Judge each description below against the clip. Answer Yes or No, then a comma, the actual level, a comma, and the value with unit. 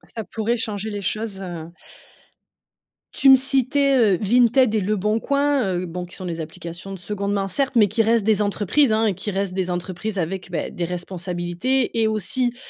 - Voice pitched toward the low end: No, high, 205 Hz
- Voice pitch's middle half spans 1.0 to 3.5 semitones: No, average, 4.2 semitones